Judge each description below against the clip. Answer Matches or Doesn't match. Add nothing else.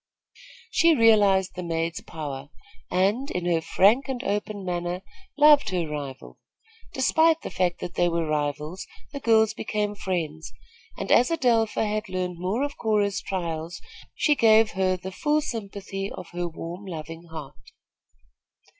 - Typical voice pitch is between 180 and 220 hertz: Matches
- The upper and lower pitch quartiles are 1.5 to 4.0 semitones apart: Doesn't match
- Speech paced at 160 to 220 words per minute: Doesn't match